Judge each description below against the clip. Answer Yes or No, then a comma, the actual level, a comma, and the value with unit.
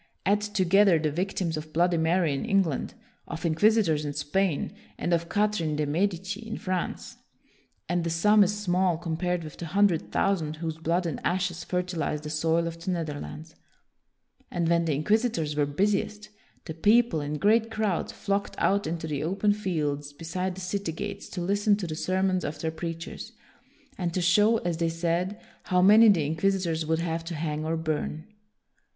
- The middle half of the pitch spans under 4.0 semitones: Yes, average, 3.5 semitones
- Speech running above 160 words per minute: Yes, average, 180 wpm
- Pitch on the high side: No, medium, 170 Hz